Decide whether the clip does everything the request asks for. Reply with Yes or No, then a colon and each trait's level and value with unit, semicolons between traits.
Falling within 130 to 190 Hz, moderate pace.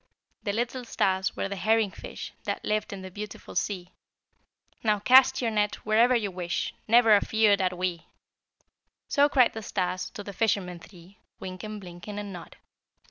No: high, 205 Hz; average, 165 wpm